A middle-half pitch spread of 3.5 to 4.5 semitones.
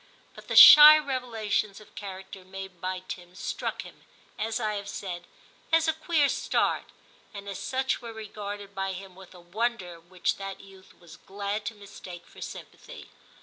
No: average, 3.1 semitones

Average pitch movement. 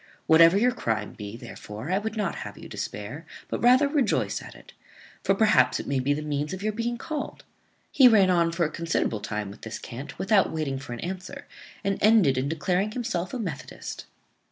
No: wide, 7.8 semitones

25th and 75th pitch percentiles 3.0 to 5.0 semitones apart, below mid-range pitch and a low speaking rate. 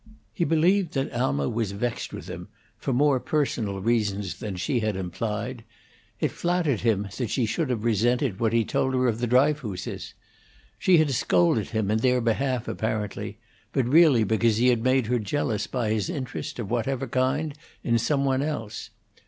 No: average, 3.8 semitones; low, 120 Hz; average, 175 wpm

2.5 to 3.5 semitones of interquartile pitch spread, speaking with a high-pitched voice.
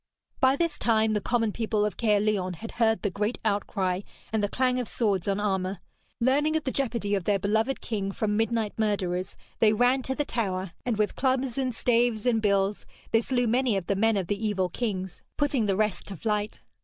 Yes: average, 3.2 semitones; high, 215 Hz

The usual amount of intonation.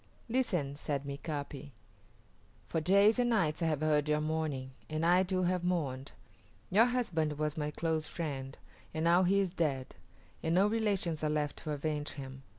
Yes: average, 3.7 semitones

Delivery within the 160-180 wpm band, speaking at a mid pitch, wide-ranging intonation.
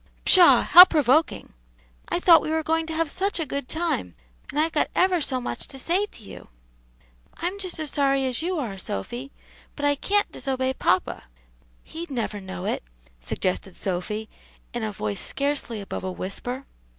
No: average, 175 wpm; very high, 275 Hz; wide, 7.2 semitones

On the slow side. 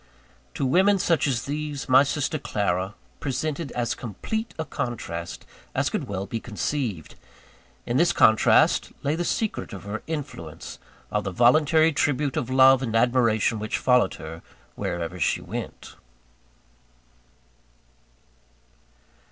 Yes: slow, 125 wpm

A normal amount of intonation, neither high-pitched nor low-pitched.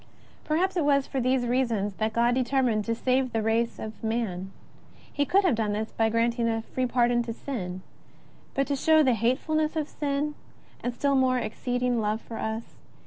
No: average, 3.4 semitones; high, 245 Hz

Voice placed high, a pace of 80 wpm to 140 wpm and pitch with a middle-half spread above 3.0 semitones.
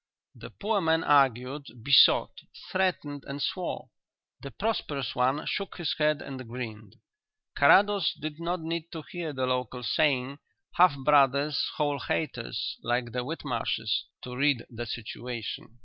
No: medium, 140 Hz; slow, 135 wpm; average, 4.0 semitones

